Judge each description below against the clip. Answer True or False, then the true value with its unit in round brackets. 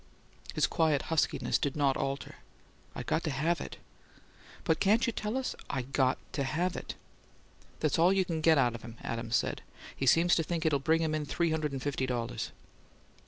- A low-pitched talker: False (155 Hz)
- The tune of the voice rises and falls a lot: False (3.6 semitones)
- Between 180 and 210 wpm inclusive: True (205 wpm)